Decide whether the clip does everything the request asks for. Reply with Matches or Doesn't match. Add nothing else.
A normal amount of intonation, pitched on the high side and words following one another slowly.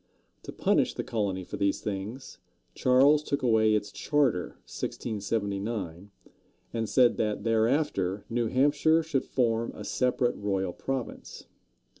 Doesn't match